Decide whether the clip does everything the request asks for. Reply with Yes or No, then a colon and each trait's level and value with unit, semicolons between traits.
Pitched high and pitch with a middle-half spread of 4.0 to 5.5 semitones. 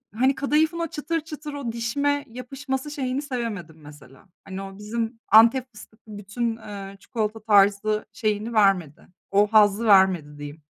Yes: high, 220 Hz; average, 4.8 semitones